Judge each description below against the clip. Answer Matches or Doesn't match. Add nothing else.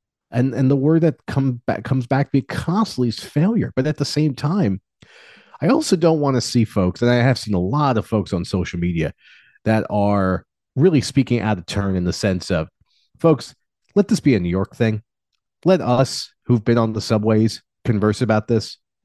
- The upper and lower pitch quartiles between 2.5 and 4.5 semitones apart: Doesn't match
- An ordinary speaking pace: Doesn't match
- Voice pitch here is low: Matches